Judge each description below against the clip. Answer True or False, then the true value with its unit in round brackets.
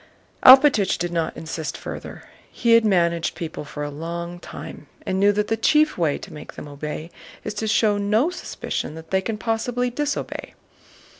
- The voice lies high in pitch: True (195 Hz)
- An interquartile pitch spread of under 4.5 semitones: False (5.4 semitones)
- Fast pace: False (175 wpm)